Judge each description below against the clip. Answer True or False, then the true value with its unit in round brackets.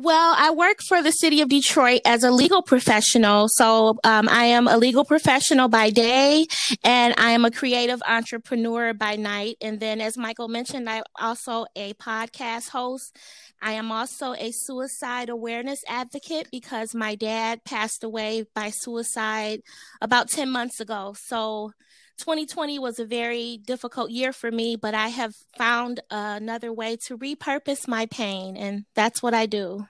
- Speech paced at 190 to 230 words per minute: False (165 wpm)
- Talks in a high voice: True (235 Hz)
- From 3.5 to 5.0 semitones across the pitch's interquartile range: False (2.7 semitones)